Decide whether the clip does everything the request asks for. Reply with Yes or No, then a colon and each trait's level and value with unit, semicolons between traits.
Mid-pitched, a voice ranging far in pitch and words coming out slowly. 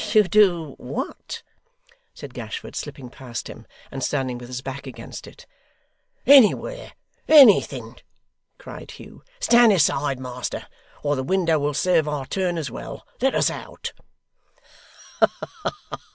Yes: medium, 150 Hz; wide, 7.2 semitones; slow, 125 wpm